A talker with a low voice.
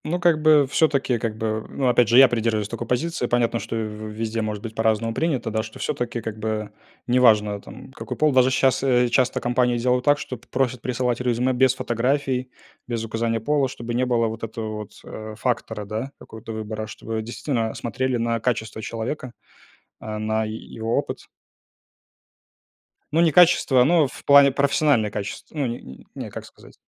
Yes: low, 120 Hz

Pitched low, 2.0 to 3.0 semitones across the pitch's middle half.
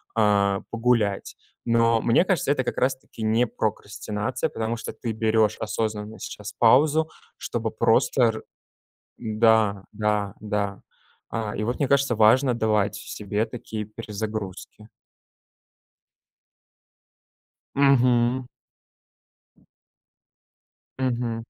Yes: low, 110 Hz; narrow, 2.5 semitones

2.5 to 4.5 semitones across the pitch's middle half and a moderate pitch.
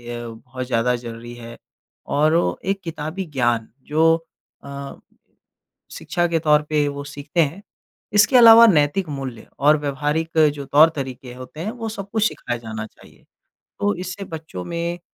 No: average, 4.9 semitones; medium, 150 Hz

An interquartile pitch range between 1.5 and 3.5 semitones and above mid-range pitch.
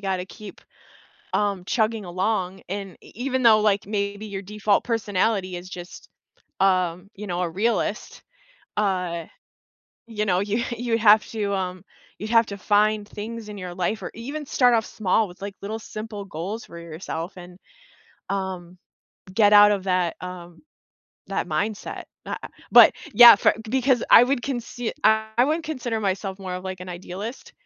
Yes: average, 3.2 semitones; high, 205 Hz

